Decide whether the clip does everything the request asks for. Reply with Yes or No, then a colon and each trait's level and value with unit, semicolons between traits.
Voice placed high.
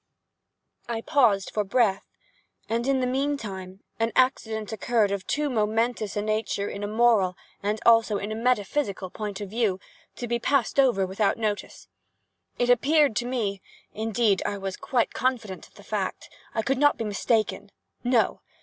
Yes: high, 220 Hz